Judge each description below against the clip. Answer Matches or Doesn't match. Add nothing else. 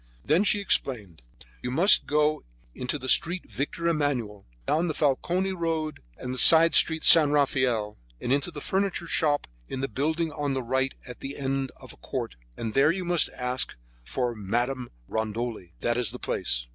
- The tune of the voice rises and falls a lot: Doesn't match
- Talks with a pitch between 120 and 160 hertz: Matches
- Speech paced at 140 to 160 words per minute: Doesn't match